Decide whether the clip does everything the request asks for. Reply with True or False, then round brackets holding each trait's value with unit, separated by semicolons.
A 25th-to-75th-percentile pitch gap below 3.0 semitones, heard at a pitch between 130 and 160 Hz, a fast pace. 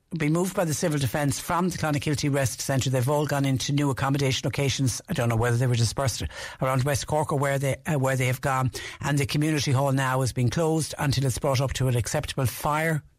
True (2.4 semitones; 140 Hz; 235 wpm)